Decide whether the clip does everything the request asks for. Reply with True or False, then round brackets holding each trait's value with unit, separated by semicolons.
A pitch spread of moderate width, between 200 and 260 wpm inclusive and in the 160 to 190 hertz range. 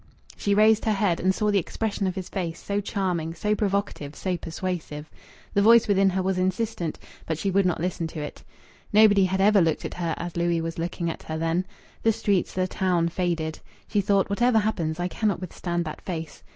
True (3.2 semitones; 205 wpm; 185 Hz)